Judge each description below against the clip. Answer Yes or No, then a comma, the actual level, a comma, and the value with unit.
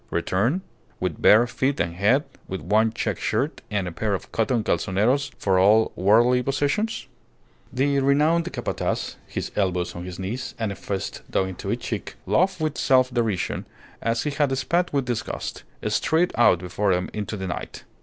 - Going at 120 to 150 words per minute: No, average, 175 wpm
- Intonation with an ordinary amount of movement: No, wide, 6.1 semitones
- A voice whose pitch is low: Yes, low, 115 Hz